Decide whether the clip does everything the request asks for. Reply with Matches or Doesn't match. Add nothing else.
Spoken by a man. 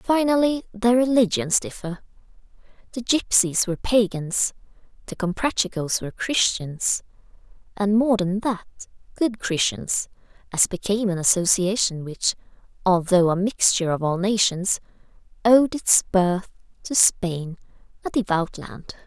Doesn't match